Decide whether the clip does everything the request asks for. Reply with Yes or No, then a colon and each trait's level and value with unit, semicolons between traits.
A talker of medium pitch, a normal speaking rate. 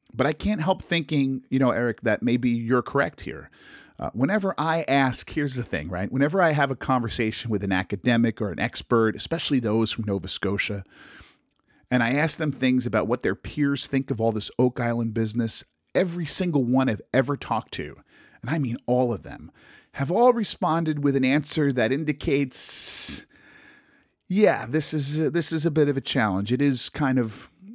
No: low, 130 Hz; average, 190 wpm